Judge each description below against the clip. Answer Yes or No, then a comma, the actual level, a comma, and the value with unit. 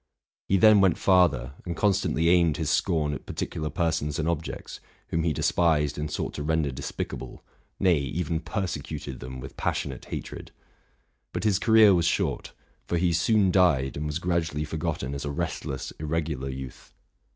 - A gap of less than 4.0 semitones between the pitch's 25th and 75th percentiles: Yes, average, 3.4 semitones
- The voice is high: No, very low, 80 Hz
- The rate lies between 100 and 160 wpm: No, average, 175 wpm